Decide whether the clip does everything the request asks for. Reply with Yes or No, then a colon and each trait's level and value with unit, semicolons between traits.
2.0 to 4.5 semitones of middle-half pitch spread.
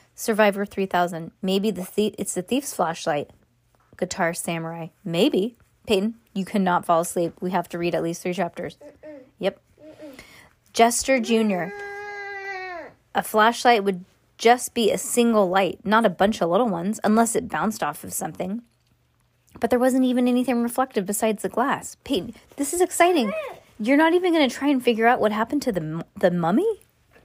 No: wide, 5.5 semitones